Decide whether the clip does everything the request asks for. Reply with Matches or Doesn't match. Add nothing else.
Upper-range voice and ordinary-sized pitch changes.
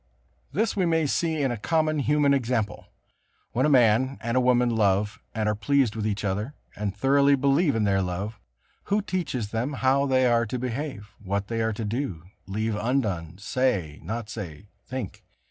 Doesn't match